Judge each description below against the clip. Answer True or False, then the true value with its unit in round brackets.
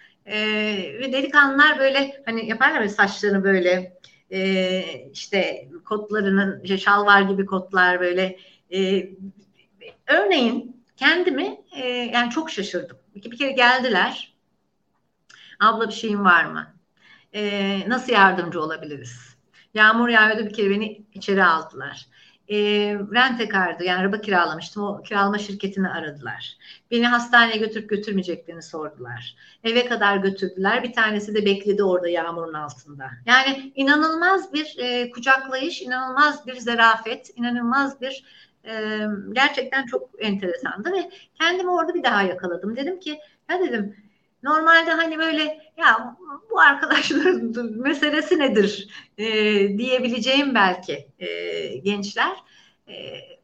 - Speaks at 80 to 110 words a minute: False (120 wpm)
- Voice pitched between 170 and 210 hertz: False (220 Hz)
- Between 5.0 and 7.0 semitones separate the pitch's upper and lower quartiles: True (5.5 semitones)